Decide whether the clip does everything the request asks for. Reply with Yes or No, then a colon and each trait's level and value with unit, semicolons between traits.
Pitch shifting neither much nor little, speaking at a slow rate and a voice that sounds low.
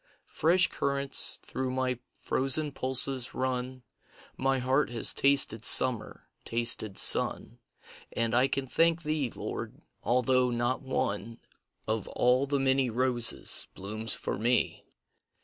No: narrow, 2.3 semitones; slow, 120 wpm; low, 130 Hz